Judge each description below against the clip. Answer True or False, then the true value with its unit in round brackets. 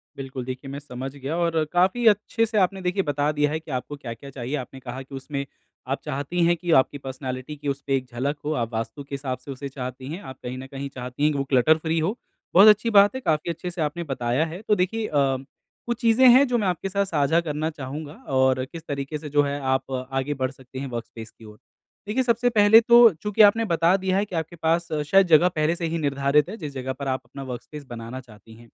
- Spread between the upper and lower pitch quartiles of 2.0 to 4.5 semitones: False (5.1 semitones)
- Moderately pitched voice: True (145 Hz)